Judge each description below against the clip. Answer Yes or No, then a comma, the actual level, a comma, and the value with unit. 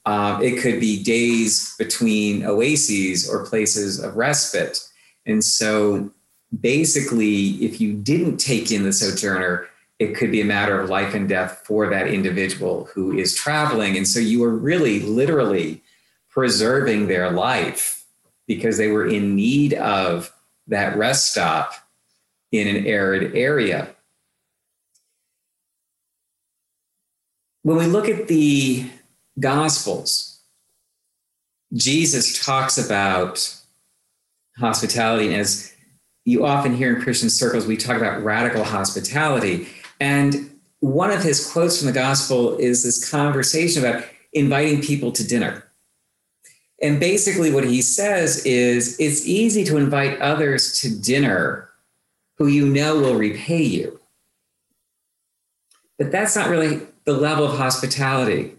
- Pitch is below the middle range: Yes, low, 125 Hz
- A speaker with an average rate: No, slow, 125 wpm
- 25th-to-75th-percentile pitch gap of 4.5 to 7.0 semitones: Yes, average, 5.2 semitones